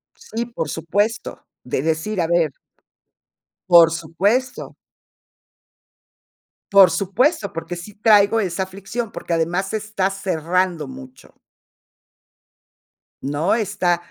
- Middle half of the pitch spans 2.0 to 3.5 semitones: No, average, 4.0 semitones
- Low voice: No, medium, 185 Hz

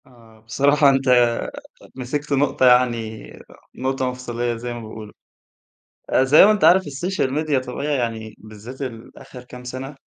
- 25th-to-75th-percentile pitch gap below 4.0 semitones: Yes, average, 3.0 semitones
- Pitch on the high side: No, low, 125 Hz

